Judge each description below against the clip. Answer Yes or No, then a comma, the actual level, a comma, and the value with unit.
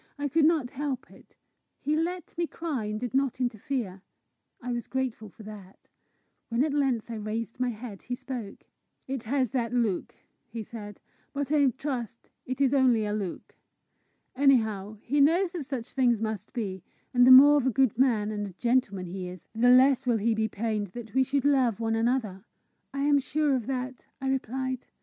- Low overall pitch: No, high, 245 Hz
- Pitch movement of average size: Yes, average, 3.7 semitones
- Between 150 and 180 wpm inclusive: No, average, 190 wpm